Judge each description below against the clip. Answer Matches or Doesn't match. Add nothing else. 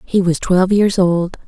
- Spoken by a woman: Matches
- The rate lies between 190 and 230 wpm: Matches